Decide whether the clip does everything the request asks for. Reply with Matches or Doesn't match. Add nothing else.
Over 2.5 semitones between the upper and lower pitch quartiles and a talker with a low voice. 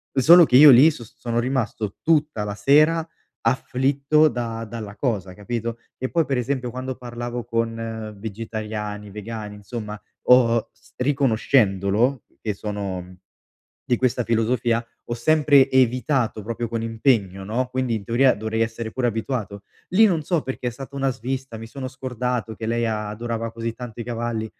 Matches